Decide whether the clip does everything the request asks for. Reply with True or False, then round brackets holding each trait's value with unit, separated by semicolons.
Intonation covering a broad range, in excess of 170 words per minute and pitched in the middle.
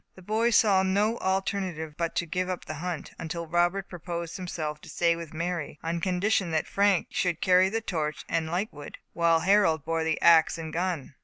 False (2.6 semitones; 200 wpm; 175 Hz)